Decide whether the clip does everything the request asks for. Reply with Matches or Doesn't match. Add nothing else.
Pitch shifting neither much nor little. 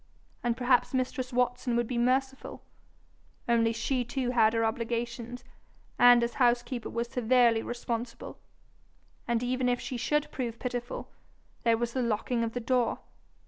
Doesn't match